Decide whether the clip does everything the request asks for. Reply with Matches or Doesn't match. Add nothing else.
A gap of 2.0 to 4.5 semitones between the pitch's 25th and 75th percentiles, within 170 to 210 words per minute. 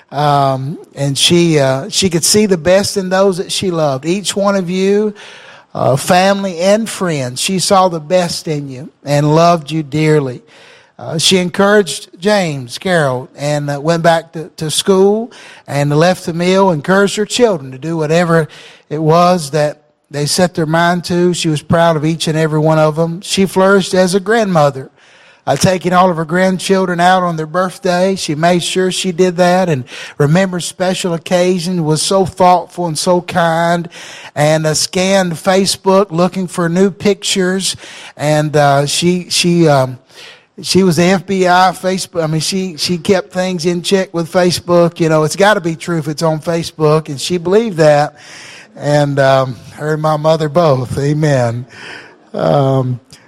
Matches